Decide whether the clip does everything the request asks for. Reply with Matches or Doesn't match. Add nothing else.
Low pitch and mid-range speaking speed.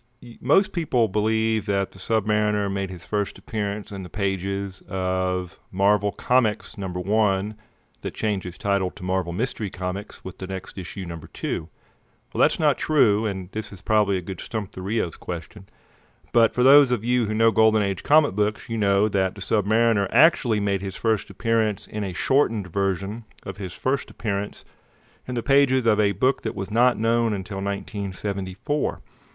Matches